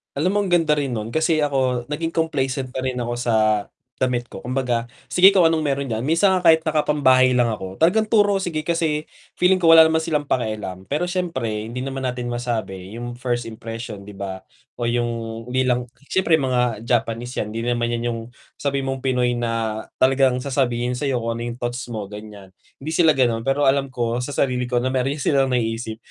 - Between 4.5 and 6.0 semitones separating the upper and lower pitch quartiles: No, average, 3.8 semitones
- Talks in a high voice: No, low, 125 Hz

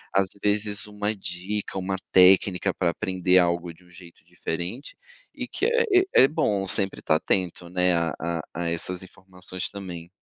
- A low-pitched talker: Yes, very low, 95 Hz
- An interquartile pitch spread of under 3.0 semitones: Yes, narrow, 2.4 semitones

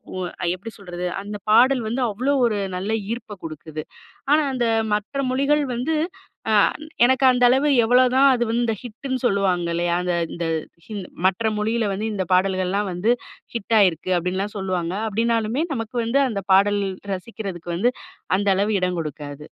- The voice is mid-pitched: No, high, 210 Hz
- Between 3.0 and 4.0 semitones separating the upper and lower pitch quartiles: No, average, 4.7 semitones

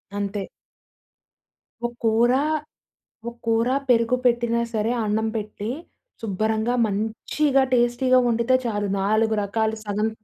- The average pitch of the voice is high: Yes, high, 225 Hz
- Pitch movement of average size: No, narrow, 2.1 semitones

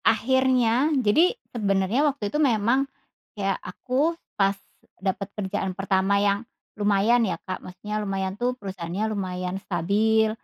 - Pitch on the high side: Yes, high, 205 Hz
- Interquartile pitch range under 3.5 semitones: No, average, 3.8 semitones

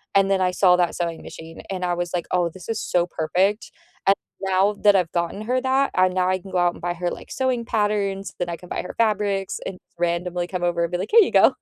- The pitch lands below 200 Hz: Yes, medium, 185 Hz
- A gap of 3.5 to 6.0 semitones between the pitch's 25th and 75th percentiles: No, narrow, 2.4 semitones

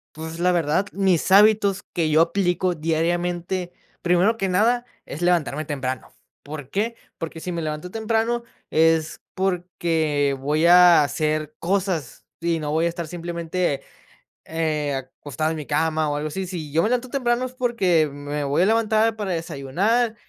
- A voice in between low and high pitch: Yes, medium, 170 Hz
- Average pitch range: Yes, average, 3.9 semitones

